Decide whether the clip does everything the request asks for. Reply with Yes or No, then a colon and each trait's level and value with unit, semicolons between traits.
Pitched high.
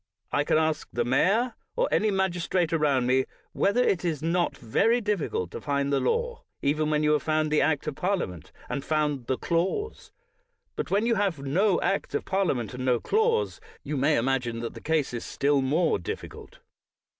No: medium, 155 Hz